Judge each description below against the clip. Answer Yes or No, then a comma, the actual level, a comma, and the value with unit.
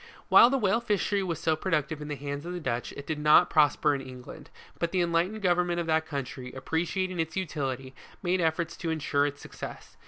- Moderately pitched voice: Yes, medium, 160 Hz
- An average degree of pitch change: Yes, average, 3.6 semitones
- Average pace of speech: No, fast, 220 wpm